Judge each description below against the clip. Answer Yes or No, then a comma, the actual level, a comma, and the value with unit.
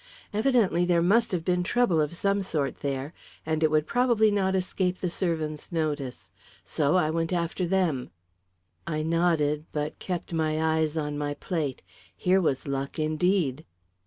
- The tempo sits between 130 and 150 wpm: No, average, 160 wpm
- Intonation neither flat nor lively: Yes, average, 3.2 semitones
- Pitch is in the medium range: Yes, medium, 165 Hz